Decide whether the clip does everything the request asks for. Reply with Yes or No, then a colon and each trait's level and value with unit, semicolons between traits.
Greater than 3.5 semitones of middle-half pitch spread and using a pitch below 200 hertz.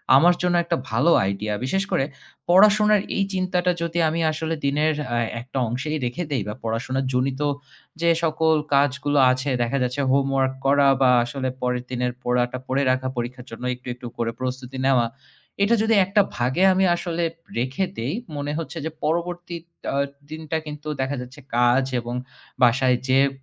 Yes: average, 4.6 semitones; low, 135 Hz